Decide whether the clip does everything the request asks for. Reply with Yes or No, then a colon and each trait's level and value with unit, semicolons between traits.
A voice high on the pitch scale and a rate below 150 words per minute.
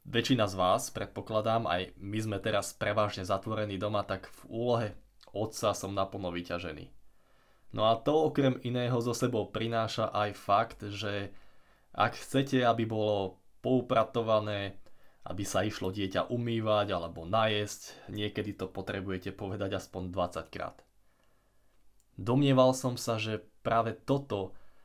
No: low, 105 Hz; average, 130 wpm